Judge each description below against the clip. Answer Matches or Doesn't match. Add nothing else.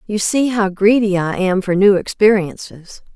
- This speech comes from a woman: Matches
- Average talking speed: Matches